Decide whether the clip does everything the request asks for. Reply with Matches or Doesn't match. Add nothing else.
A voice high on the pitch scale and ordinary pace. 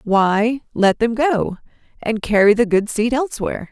Matches